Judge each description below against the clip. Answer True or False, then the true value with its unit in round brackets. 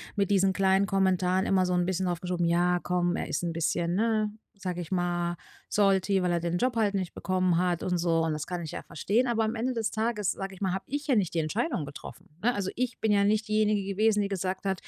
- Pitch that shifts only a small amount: False (3.0 semitones)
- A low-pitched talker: False (190 Hz)